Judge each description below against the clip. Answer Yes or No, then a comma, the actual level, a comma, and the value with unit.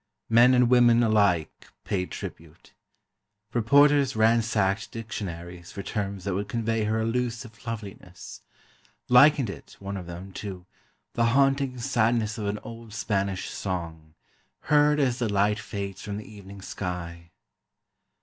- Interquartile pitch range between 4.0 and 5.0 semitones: No, average, 3.5 semitones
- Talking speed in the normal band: No, slow, 130 wpm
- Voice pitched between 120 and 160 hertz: No, low, 110 Hz